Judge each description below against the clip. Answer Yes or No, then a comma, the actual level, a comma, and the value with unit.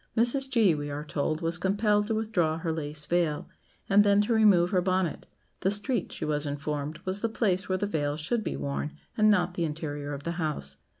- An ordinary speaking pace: No, fast, 215 wpm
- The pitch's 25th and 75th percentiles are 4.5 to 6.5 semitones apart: Yes, wide, 5.5 semitones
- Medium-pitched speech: Yes, medium, 175 Hz